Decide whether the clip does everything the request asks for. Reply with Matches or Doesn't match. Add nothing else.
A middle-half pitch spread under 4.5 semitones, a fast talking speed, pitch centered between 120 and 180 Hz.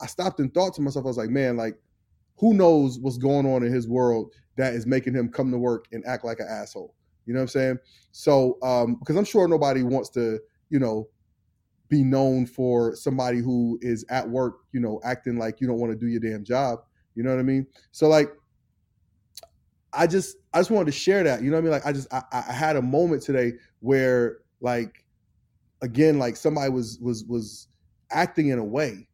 Matches